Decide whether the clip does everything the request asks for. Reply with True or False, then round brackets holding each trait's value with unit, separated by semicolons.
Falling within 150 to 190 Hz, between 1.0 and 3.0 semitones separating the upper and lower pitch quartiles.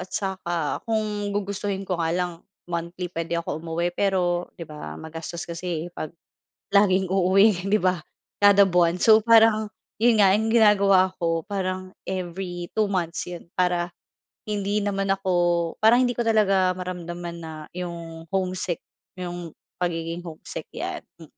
True (185 Hz; 2.7 semitones)